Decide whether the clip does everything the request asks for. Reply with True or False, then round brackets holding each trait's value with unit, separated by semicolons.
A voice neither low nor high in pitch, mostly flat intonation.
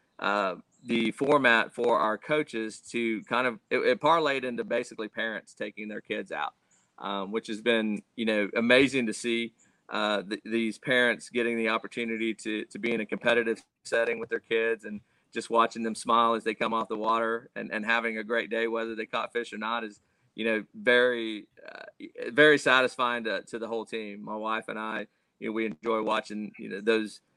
False (115 Hz; 1.3 semitones)